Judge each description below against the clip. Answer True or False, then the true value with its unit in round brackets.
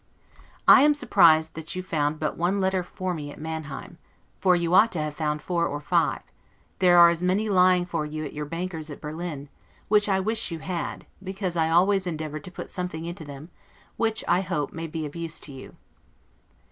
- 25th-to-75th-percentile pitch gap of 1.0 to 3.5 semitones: True (3.0 semitones)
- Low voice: False (170 Hz)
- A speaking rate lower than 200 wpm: False (205 wpm)